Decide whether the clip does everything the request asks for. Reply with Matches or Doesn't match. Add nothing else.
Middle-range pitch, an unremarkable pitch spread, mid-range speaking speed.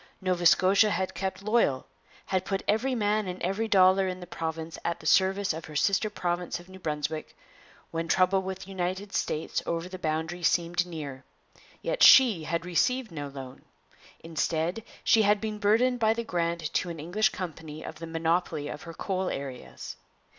Matches